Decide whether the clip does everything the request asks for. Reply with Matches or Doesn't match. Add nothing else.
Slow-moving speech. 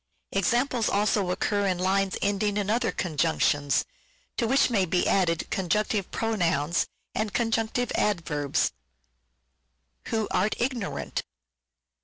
Matches